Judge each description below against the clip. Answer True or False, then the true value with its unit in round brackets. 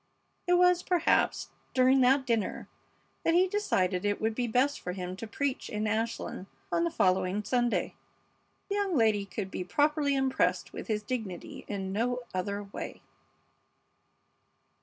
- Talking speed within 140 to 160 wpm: True (150 wpm)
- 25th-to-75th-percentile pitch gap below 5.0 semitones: False (5.6 semitones)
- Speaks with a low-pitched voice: False (225 Hz)